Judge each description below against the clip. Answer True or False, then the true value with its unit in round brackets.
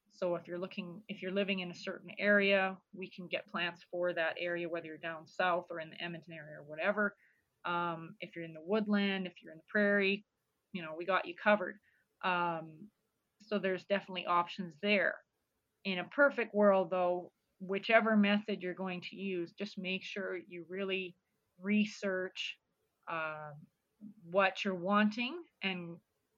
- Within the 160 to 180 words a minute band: True (170 wpm)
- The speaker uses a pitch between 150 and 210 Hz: True (185 Hz)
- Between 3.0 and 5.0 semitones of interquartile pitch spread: False (2.6 semitones)